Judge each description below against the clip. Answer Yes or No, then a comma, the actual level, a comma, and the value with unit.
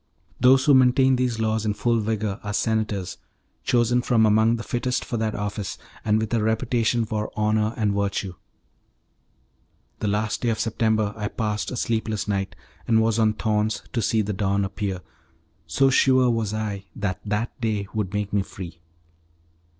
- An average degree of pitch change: No, narrow, 2.0 semitones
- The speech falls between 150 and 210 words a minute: Yes, average, 170 wpm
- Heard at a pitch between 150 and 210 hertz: No, low, 110 Hz